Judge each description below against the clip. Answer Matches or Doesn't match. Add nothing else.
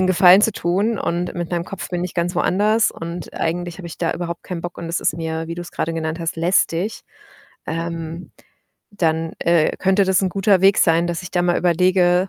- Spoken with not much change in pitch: Matches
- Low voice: Doesn't match